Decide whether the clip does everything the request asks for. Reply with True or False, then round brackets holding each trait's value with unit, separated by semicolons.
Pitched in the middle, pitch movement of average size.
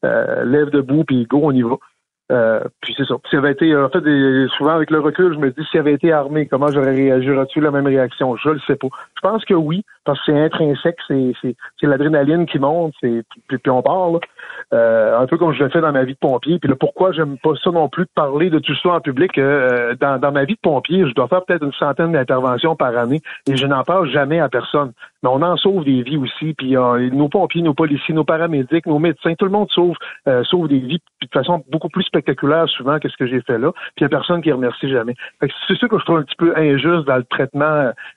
True (150 Hz; 3.5 semitones)